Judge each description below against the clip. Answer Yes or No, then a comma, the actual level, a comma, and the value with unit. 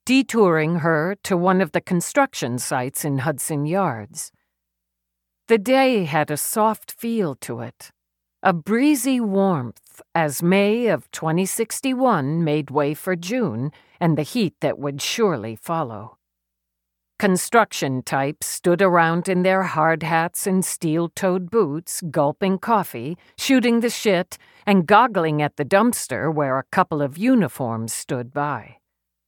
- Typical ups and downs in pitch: No, wide, 6.0 semitones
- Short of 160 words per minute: Yes, slow, 135 wpm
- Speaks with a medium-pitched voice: Yes, medium, 165 Hz